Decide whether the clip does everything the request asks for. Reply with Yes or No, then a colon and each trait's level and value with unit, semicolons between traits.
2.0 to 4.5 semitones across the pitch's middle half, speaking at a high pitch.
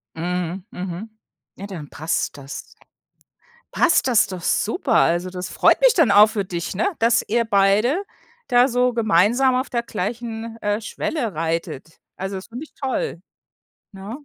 No: average, 5.0 semitones; high, 210 Hz